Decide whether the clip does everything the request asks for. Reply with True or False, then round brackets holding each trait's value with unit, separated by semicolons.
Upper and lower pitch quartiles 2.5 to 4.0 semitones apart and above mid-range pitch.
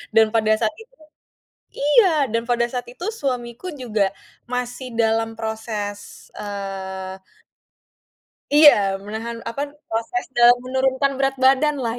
True (3.2 semitones; 235 Hz)